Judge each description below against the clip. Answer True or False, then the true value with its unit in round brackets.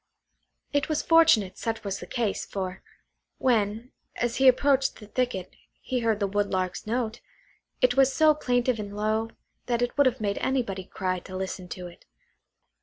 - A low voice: False (225 Hz)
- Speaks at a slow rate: False (170 wpm)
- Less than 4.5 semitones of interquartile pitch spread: True (4.1 semitones)